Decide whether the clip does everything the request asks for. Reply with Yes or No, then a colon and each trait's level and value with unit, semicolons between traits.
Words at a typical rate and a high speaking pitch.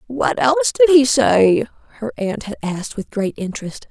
Yes: average, 185 wpm; high, 240 Hz